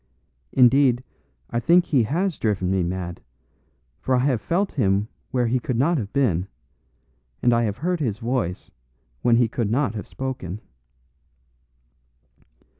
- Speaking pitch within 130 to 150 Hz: No, low, 120 Hz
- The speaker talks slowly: No, average, 145 wpm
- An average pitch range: Yes, average, 4.7 semitones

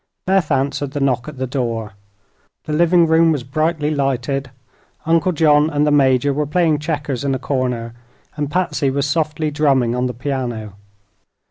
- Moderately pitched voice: Yes, medium, 145 Hz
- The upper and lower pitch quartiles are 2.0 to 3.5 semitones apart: Yes, average, 2.9 semitones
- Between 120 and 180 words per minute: Yes, average, 165 wpm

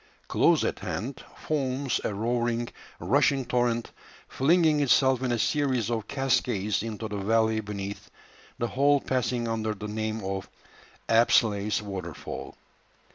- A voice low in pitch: Yes, low, 115 Hz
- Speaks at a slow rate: Yes, slow, 130 wpm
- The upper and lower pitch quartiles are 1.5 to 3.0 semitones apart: No, average, 3.4 semitones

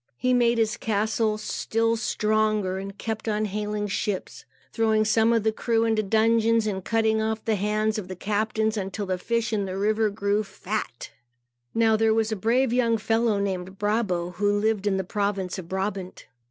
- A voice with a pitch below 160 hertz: No, high, 215 Hz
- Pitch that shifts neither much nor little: No, narrow, 1.8 semitones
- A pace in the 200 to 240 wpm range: No, average, 180 wpm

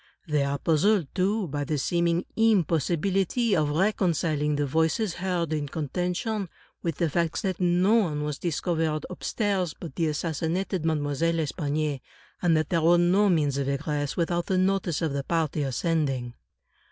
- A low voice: No, medium, 165 Hz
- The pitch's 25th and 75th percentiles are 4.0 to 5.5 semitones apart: No, average, 3.5 semitones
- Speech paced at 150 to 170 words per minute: Yes, average, 160 wpm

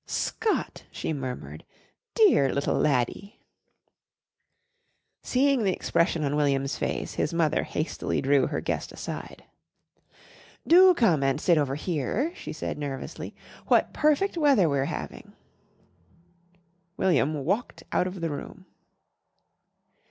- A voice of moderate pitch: Yes, medium, 160 Hz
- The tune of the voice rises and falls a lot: Yes, wide, 8.7 semitones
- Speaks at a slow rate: Yes, slow, 115 wpm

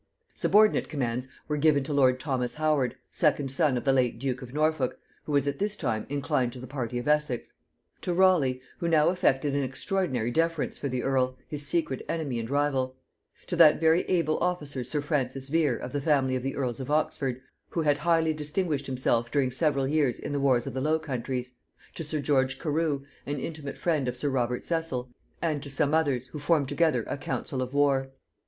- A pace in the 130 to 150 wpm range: No, fast, 205 wpm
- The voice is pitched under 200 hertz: Yes, medium, 140 Hz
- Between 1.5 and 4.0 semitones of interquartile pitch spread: Yes, average, 3.2 semitones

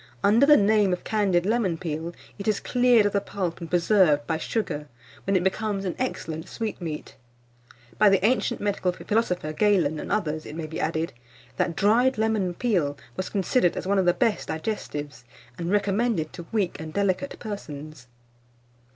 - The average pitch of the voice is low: No, high, 190 Hz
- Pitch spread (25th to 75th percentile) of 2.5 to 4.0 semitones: No, average, 4.7 semitones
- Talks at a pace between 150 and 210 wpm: Yes, average, 170 wpm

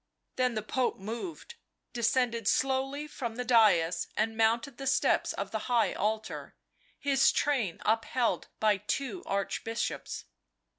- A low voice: No, high, 235 Hz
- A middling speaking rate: No, slow, 130 wpm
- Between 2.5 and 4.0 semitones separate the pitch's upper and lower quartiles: Yes, average, 3.4 semitones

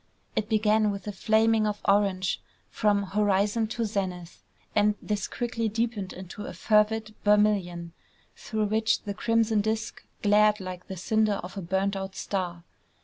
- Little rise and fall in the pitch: Yes, narrow, 2.1 semitones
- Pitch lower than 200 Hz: No, high, 210 Hz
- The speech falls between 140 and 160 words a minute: Yes, average, 150 wpm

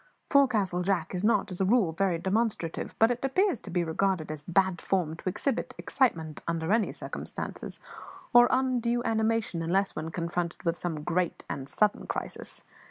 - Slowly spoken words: No, average, 165 wpm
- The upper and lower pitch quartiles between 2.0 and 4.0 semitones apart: No, average, 5.2 semitones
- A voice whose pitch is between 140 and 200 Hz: Yes, high, 190 Hz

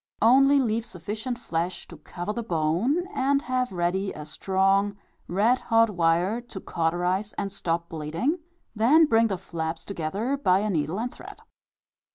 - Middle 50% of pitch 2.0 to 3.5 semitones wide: No, wide, 5.5 semitones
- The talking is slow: No, average, 155 wpm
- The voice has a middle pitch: No, high, 200 Hz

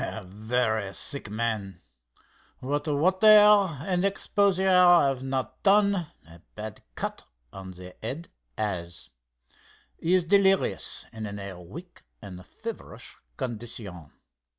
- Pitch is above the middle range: No, low, 125 Hz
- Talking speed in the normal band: No, slow, 115 wpm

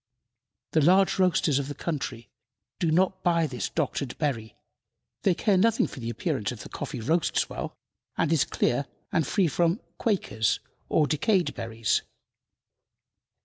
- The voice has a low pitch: No, medium, 160 Hz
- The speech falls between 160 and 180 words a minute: No, average, 145 wpm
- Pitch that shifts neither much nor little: No, wide, 5.9 semitones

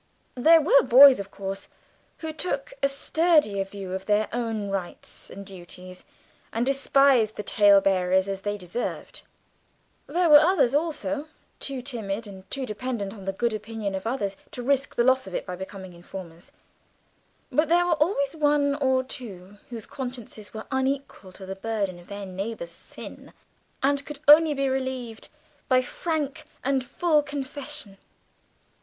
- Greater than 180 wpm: No, average, 155 wpm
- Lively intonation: Yes, wide, 6.1 semitones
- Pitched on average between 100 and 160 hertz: No, high, 240 Hz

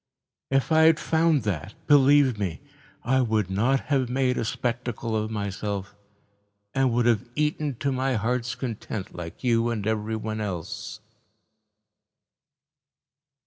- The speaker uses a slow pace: Yes, slow, 125 wpm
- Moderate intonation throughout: Yes, average, 3.9 semitones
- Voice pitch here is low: Yes, low, 115 Hz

